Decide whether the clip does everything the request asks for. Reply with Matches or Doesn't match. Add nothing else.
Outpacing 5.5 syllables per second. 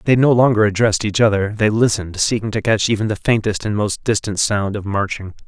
Matches